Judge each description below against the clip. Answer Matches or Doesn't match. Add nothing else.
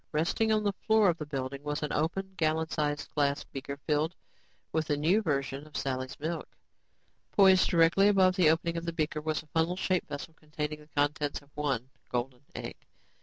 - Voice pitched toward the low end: Doesn't match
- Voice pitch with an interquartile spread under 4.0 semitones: Matches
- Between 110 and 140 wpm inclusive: Doesn't match